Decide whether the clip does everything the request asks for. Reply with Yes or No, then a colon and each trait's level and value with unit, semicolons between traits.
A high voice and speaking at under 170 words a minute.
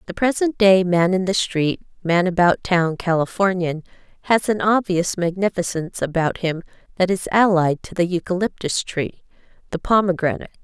No: medium, 180 Hz; average, 145 wpm